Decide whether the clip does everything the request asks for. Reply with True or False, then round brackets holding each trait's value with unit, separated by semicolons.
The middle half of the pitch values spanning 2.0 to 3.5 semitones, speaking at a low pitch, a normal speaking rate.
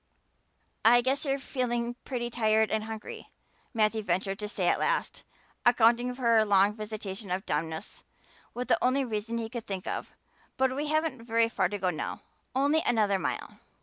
False (3.2 semitones; 225 Hz; 175 wpm)